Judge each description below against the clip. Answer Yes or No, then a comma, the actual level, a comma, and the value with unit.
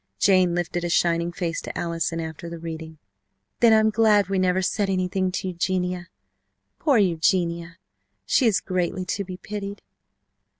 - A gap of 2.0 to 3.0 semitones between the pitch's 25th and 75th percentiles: Yes, narrow, 2.5 semitones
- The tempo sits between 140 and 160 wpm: Yes, average, 155 wpm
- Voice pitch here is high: No, medium, 180 Hz